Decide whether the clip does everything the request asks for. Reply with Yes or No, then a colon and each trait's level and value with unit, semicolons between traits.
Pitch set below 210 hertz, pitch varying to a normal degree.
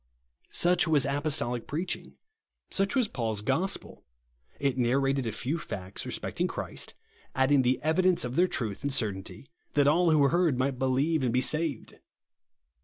Yes: medium, 140 Hz; average, 4.2 semitones